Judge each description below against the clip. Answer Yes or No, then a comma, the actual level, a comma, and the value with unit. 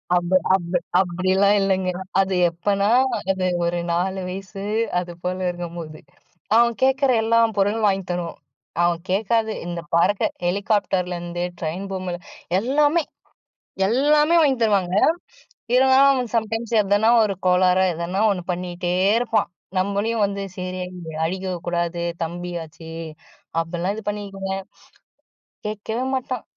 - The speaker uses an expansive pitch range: No, average, 3.7 semitones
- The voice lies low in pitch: No, high, 190 Hz